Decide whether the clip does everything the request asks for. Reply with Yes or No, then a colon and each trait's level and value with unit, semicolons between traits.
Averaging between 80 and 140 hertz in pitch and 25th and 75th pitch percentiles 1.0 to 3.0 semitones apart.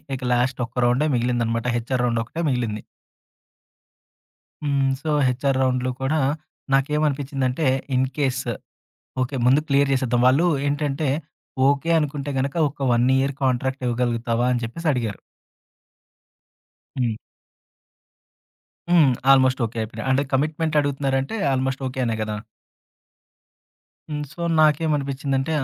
Yes: low, 135 Hz; narrow, 2.4 semitones